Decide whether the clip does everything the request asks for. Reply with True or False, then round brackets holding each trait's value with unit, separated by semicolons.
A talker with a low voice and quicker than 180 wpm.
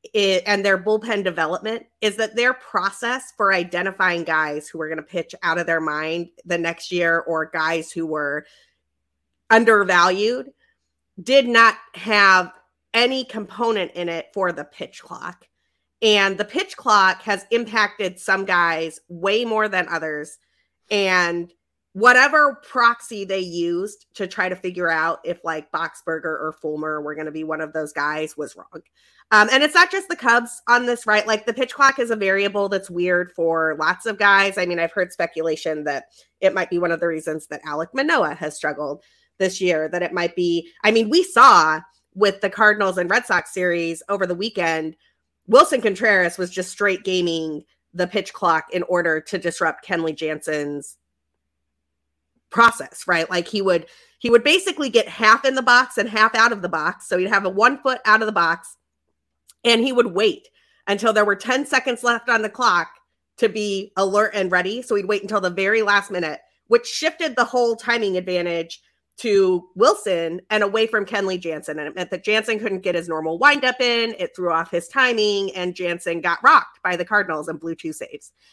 False (190 Hz; 190 wpm)